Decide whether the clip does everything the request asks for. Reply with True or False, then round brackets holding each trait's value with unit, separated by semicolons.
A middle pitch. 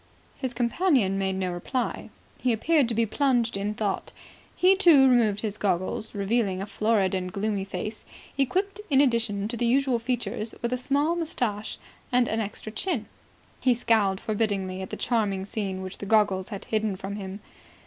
False (220 Hz)